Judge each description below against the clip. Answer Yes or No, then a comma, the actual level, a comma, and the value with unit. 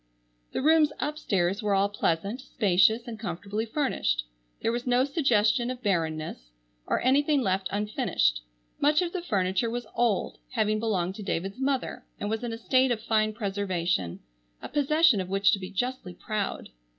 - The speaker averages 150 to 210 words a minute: Yes, average, 165 wpm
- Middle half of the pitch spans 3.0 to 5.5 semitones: Yes, average, 4.7 semitones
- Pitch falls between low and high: No, high, 215 Hz